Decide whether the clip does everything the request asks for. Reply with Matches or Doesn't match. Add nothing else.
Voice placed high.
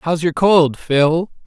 Doesn't match